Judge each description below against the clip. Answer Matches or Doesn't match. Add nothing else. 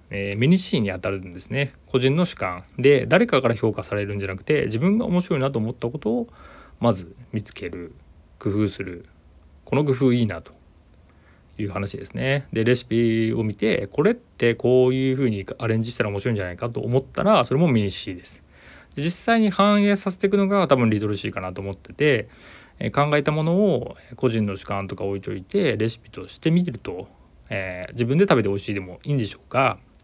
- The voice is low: Matches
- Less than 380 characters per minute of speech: Doesn't match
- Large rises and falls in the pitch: Matches